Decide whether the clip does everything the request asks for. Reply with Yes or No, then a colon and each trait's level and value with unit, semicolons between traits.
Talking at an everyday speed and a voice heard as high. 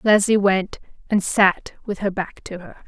Yes: average, 190 wpm; high, 195 Hz